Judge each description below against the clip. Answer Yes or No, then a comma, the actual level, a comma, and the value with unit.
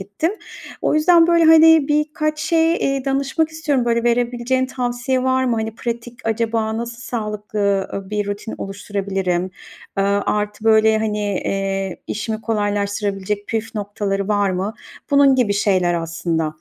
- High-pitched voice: Yes, high, 220 Hz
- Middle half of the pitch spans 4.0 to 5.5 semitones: Yes, average, 4.4 semitones